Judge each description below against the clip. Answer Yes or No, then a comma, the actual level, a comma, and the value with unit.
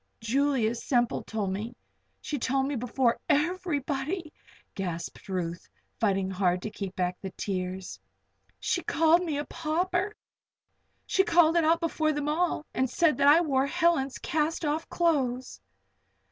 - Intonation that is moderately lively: No, wide, 7.1 semitones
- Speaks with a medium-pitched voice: No, very high, 280 Hz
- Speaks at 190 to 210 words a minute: No, average, 145 wpm